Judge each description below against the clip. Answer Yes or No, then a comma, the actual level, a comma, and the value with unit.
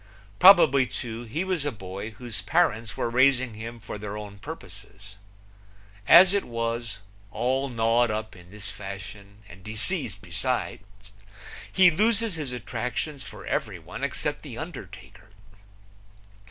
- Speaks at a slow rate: Yes, slow, 130 wpm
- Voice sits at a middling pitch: No, low, 115 Hz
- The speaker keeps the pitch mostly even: No, average, 4.8 semitones